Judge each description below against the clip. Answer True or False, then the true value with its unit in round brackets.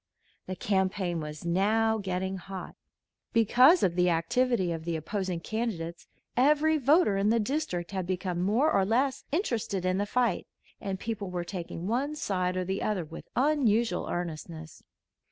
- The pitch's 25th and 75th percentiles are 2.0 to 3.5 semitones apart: False (4.8 semitones)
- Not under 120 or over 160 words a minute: True (155 wpm)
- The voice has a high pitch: True (195 Hz)